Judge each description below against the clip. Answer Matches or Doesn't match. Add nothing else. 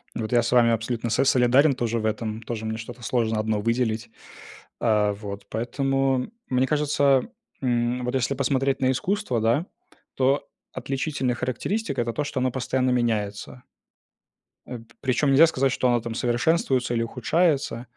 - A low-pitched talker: Matches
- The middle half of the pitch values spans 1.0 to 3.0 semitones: Matches